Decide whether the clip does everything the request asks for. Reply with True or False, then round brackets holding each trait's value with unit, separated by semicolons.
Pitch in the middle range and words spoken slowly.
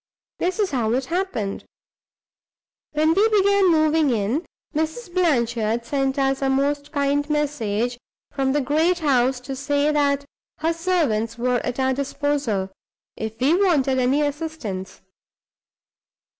False (280 Hz; 130 wpm)